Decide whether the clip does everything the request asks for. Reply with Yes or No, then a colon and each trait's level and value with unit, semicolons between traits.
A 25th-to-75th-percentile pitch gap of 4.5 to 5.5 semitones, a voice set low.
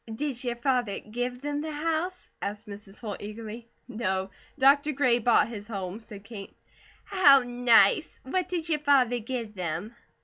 No: average, 5.2 semitones; high, 240 Hz